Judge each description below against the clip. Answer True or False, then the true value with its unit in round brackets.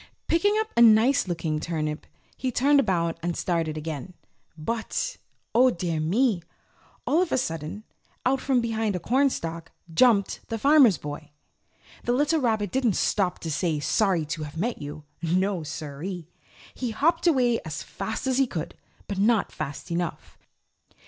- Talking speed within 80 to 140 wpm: False (160 wpm)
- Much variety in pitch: True (7.5 semitones)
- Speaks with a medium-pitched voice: False (200 Hz)